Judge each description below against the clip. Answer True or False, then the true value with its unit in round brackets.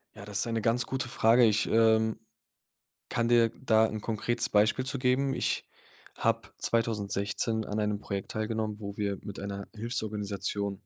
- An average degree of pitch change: False (2.2 semitones)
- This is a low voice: True (110 Hz)